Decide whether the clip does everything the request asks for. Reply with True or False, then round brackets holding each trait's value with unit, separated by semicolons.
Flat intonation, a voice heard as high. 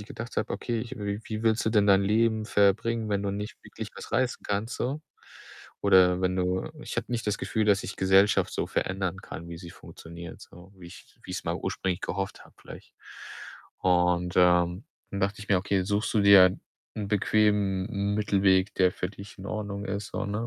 False (2.3 semitones; 100 Hz)